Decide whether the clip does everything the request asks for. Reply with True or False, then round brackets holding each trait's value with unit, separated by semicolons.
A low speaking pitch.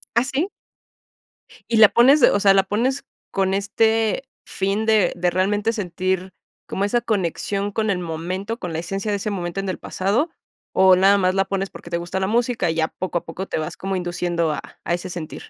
False (195 Hz)